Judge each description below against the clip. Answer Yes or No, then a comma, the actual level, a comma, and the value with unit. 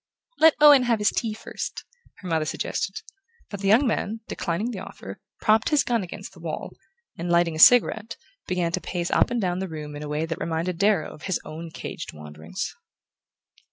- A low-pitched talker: No, medium, 185 Hz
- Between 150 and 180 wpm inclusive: No, average, 195 wpm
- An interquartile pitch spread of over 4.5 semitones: Yes, average, 5.1 semitones